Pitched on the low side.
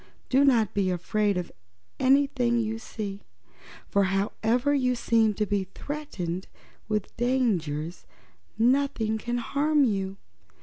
No: high, 225 Hz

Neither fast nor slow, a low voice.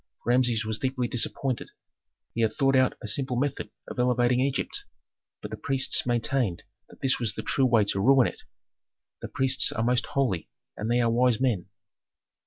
Yes: average, 180 wpm; low, 125 Hz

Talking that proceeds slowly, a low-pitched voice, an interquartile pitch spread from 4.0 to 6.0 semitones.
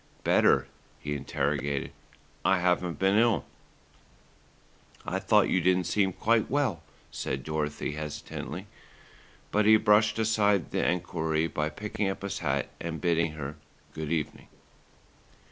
Yes: slow, 130 wpm; very low, 85 Hz; average, 5.1 semitones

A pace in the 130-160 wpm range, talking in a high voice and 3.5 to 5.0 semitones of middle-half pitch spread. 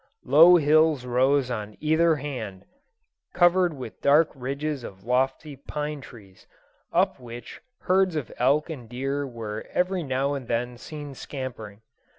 No: average, 140 wpm; low, 135 Hz; average, 3.9 semitones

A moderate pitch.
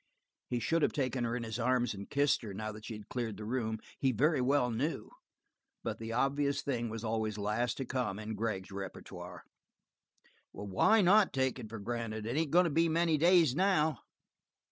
No: low, 120 Hz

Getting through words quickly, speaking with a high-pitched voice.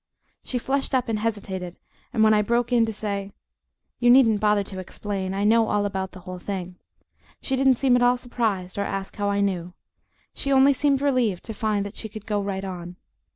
Yes: fast, 210 wpm; high, 210 Hz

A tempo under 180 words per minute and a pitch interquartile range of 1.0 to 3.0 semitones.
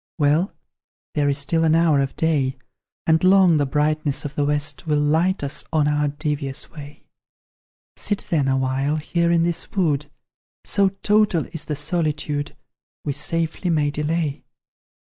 Yes: average, 150 wpm; narrow, 2.5 semitones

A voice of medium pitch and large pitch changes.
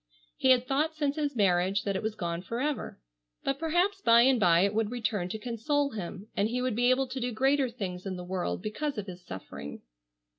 No: high, 230 Hz; wide, 5.9 semitones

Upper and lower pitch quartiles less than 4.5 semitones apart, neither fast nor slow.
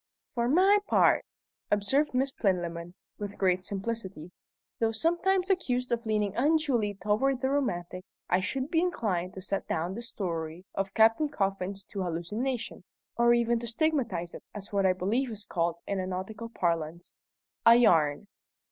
No: wide, 5.5 semitones; average, 155 wpm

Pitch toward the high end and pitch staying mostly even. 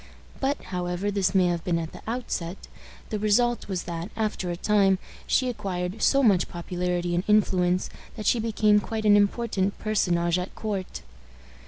No: high, 195 Hz; average, 3.2 semitones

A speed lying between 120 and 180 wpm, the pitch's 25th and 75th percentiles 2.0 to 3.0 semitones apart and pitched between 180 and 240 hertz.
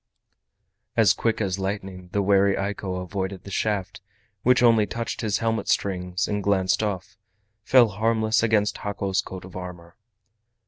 No: average, 145 wpm; narrow, 2.6 semitones; low, 100 Hz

